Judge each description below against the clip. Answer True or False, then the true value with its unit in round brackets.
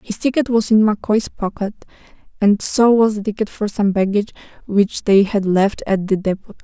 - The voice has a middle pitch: False (210 Hz)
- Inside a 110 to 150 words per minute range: False (190 wpm)